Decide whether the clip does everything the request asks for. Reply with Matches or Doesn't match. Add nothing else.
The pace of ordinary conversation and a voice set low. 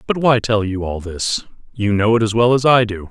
Doesn't match